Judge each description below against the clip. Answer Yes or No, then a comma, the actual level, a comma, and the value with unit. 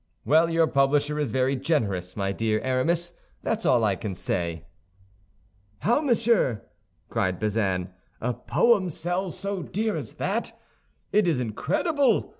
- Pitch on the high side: No, medium, 140 Hz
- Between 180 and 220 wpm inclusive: No, slow, 135 wpm